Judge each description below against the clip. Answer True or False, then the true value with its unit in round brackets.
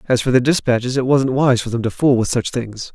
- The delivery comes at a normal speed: False (285 wpm)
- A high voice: False (125 Hz)